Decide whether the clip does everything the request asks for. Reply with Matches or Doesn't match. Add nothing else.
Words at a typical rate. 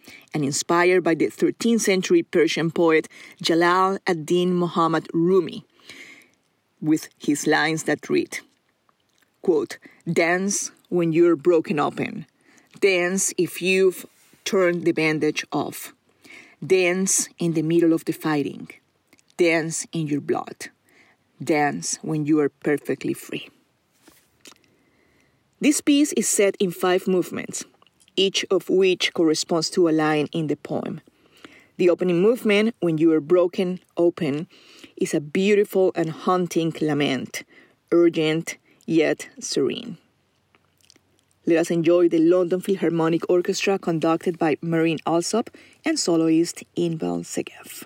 Doesn't match